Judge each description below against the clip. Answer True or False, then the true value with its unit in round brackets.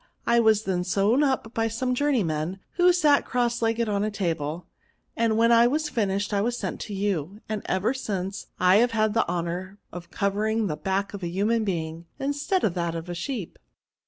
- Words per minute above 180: True (200 wpm)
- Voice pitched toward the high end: True (205 Hz)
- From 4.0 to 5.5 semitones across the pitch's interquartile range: True (4.4 semitones)